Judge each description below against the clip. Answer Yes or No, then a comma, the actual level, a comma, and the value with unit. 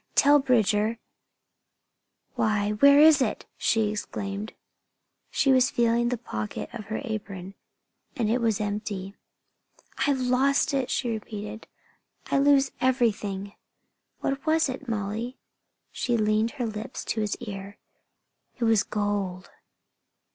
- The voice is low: No, high, 225 Hz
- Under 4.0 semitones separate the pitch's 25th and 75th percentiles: Yes, average, 3.6 semitones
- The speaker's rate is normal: No, slow, 130 wpm